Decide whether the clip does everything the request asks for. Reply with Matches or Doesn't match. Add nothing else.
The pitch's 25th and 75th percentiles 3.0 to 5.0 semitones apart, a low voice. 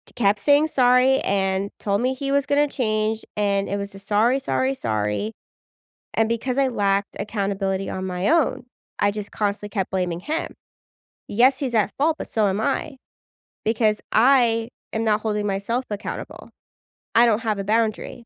Doesn't match